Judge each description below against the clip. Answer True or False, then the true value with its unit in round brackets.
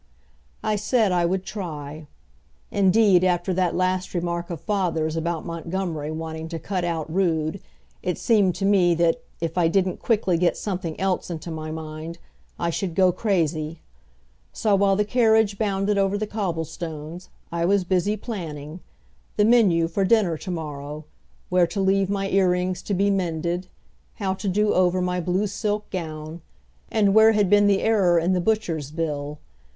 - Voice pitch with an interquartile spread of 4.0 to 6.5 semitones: False (3.2 semitones)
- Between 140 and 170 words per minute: True (165 wpm)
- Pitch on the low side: False (180 Hz)